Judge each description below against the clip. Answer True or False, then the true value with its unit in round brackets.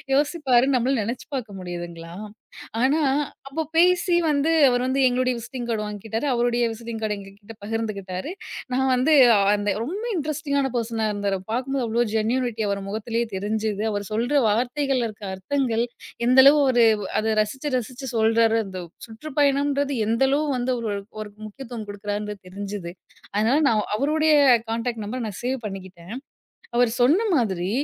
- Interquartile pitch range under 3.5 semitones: False (4.2 semitones)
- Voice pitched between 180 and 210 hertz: False (235 Hz)